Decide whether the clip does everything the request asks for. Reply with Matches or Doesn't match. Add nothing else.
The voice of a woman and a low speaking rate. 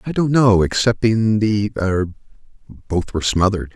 Doesn't match